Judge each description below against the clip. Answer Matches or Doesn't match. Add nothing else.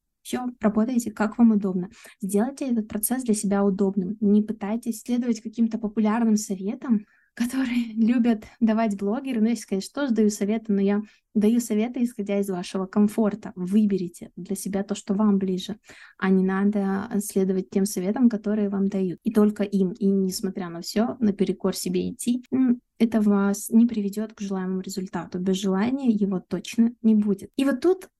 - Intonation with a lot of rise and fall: Doesn't match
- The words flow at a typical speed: Doesn't match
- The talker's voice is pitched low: Doesn't match